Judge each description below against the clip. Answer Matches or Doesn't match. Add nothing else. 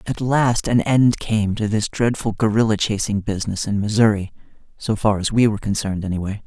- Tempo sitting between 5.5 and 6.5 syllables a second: Matches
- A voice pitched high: Doesn't match